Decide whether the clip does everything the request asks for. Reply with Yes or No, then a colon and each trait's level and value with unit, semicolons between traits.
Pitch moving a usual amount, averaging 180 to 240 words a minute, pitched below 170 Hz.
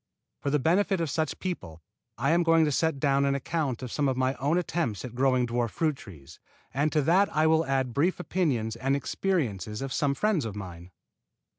Yes: average, 4.9 semitones; fast, 205 wpm; medium, 140 Hz